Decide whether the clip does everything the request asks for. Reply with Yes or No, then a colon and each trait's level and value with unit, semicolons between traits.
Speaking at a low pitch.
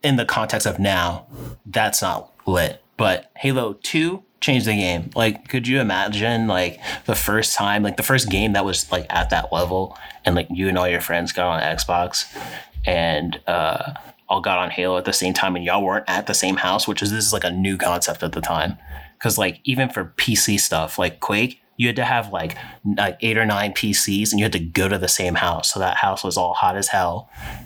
Yes: low, 100 Hz